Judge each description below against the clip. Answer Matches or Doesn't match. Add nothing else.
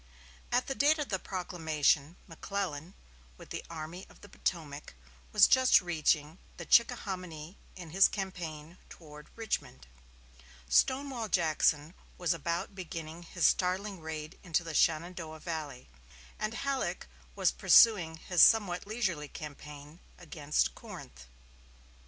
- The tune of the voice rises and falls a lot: Doesn't match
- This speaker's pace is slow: Matches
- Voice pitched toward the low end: Doesn't match